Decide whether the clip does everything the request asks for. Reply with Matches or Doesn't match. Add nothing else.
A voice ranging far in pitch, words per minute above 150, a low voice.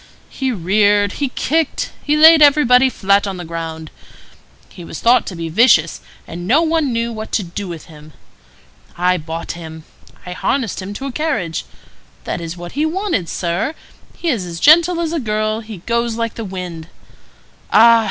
Doesn't match